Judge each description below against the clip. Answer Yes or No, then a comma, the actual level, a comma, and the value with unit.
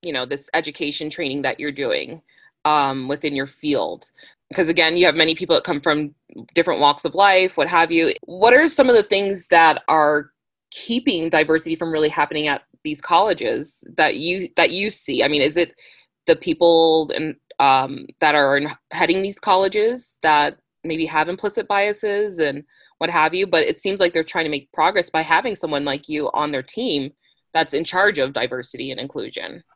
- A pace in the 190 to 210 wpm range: Yes, average, 195 wpm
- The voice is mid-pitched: Yes, medium, 165 Hz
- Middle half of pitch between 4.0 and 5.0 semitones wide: Yes, average, 4.7 semitones